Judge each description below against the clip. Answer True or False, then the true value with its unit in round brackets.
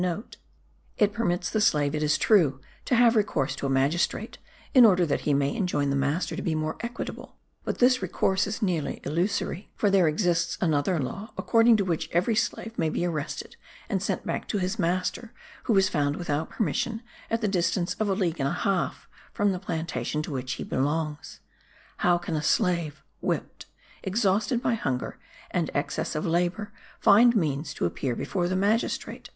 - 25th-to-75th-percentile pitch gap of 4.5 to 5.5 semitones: True (5.2 semitones)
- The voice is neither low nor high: True (175 Hz)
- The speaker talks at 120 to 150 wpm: False (185 wpm)